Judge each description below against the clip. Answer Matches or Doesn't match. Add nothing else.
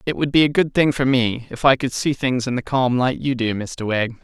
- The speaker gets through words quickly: Matches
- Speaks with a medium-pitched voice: Doesn't match